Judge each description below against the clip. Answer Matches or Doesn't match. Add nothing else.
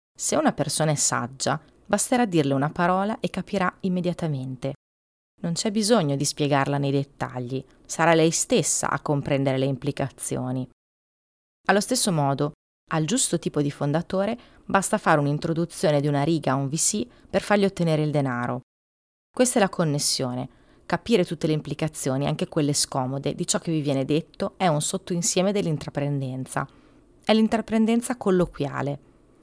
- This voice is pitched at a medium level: Matches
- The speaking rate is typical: Matches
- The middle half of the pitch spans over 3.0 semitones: Matches